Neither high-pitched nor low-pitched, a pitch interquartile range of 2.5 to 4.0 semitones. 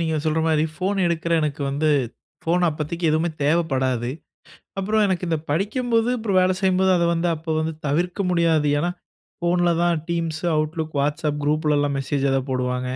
Yes: medium, 160 Hz; average, 2.9 semitones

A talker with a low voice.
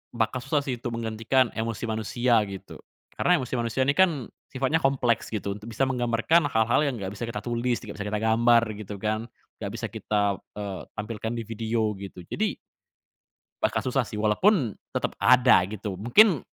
Yes: low, 115 Hz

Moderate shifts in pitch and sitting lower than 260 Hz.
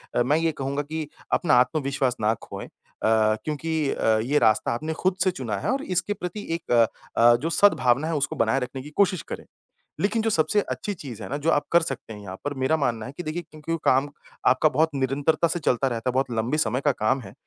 Yes: average, 4.7 semitones; medium, 140 Hz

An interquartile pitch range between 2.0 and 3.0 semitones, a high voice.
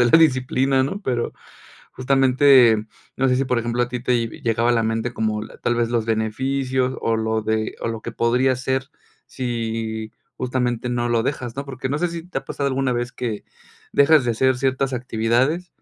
No: narrow, 2.5 semitones; low, 125 Hz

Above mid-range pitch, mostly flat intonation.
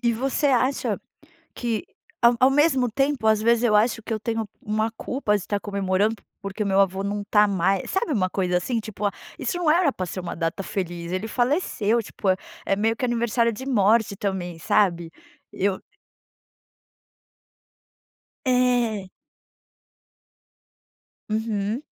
No: high, 215 Hz; average, 3.6 semitones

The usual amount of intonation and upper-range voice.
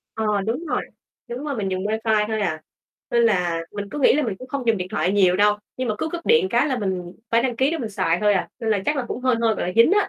Yes: average, 4.5 semitones; high, 225 Hz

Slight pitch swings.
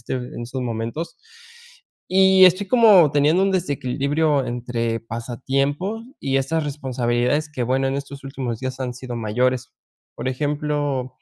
No: average, 3.3 semitones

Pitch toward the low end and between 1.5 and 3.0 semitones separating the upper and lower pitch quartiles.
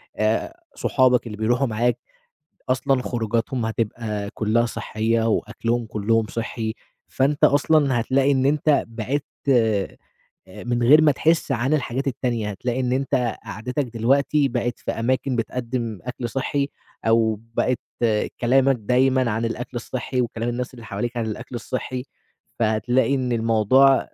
Yes: low, 120 Hz; narrow, 2.6 semitones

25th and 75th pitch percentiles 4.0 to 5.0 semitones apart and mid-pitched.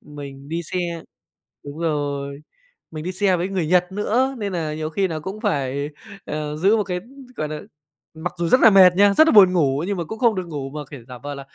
Yes: average, 4.6 semitones; medium, 170 Hz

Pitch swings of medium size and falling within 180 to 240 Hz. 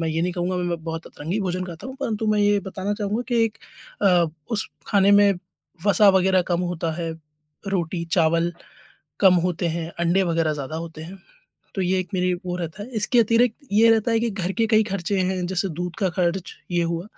Yes: average, 3.2 semitones; medium, 185 Hz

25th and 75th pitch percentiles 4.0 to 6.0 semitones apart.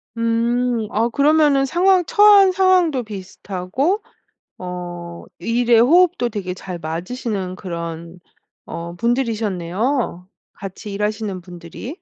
No: wide, 7.0 semitones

